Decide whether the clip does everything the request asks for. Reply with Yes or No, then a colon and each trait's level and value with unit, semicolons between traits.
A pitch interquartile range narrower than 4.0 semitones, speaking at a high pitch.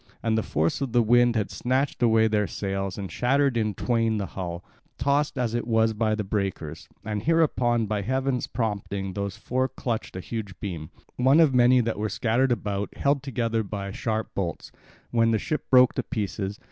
No: average, 3.6 semitones; low, 110 Hz